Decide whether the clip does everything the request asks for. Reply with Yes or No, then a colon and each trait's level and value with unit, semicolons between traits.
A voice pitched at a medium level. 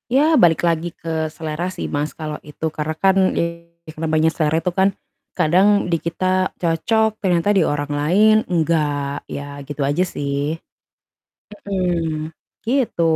Yes: medium, 165 Hz